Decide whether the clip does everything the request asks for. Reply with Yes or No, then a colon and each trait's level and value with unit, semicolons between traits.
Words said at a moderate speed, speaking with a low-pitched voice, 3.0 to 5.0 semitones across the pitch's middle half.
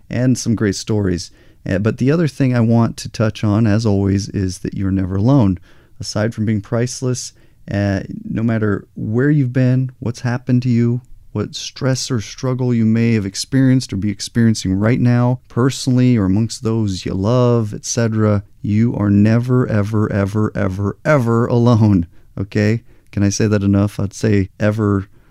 Yes: average, 170 wpm; low, 110 Hz; average, 3.3 semitones